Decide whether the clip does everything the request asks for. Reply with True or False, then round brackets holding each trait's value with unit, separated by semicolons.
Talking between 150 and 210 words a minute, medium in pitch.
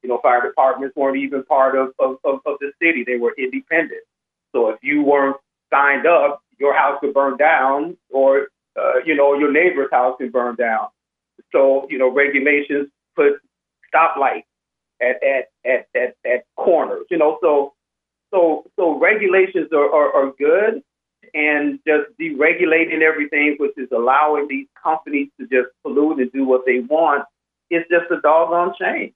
True (165 wpm; 145 Hz)